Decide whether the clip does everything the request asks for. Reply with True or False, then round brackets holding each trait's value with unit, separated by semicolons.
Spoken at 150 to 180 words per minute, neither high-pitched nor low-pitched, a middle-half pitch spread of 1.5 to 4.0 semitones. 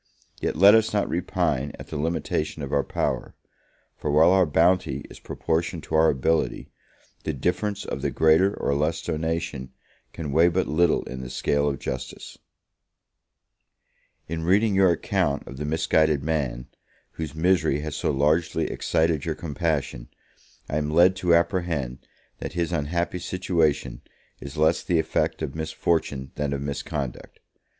False (155 wpm; 80 Hz; 3.1 semitones)